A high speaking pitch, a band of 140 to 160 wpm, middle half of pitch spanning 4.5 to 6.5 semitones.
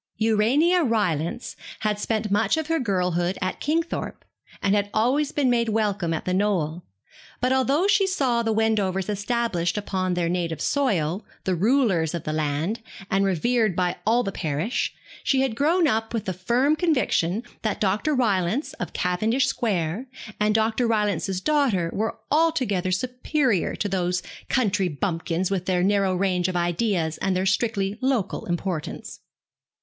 Yes: high, 205 Hz; average, 155 wpm; average, 5.1 semitones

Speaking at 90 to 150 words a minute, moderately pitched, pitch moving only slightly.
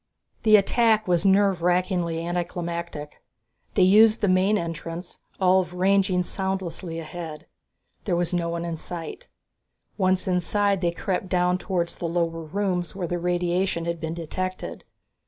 Yes: average, 140 wpm; medium, 180 Hz; narrow, 2.0 semitones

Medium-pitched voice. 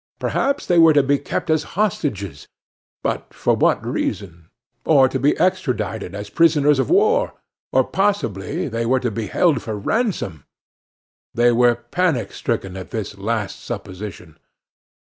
No: low, 120 Hz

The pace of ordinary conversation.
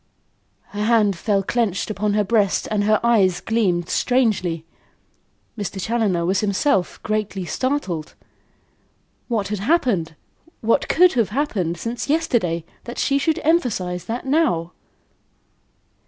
No: slow, 125 wpm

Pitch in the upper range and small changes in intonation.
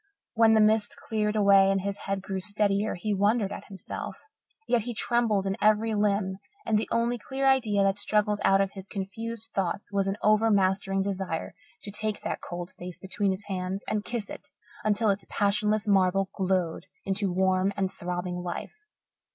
Yes: high, 200 Hz; narrow, 1.9 semitones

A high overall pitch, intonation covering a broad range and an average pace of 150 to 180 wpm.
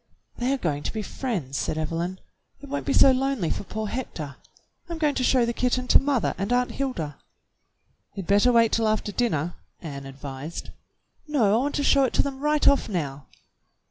No: high, 225 Hz; wide, 8.2 semitones; average, 200 wpm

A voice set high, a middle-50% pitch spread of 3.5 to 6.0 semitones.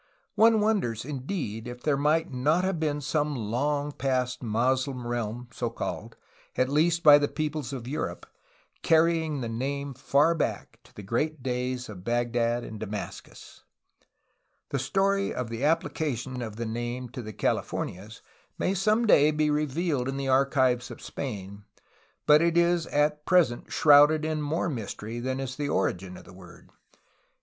No: low, 135 Hz; average, 4.3 semitones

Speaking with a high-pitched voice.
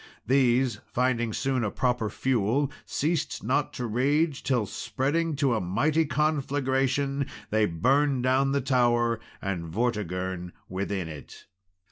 No: low, 125 Hz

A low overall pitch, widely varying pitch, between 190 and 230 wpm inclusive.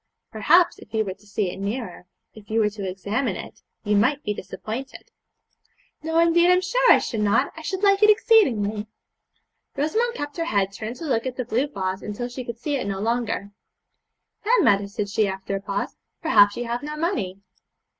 No: high, 230 Hz; wide, 7.2 semitones; average, 200 wpm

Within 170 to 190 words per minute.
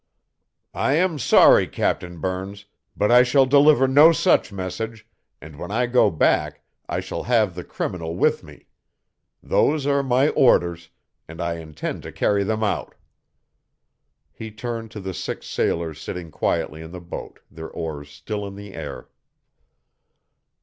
No: average, 150 wpm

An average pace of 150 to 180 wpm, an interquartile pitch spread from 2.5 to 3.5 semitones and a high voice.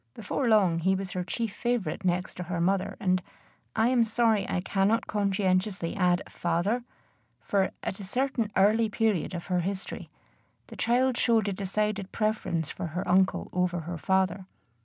Yes: average, 165 wpm; average, 3.1 semitones; high, 195 Hz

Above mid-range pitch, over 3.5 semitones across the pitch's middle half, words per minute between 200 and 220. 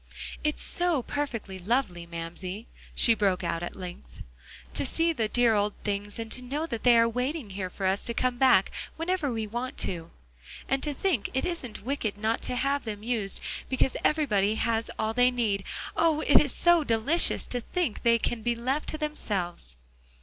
No: high, 235 Hz; average, 5.2 semitones; average, 185 wpm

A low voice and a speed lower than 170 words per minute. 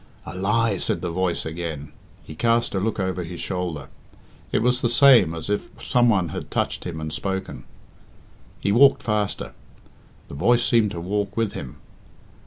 No: very low, 95 Hz; average, 175 wpm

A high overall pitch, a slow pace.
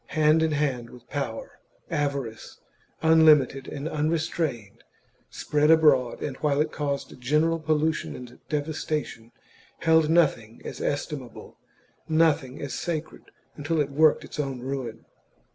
No: medium, 150 Hz; slow, 125 wpm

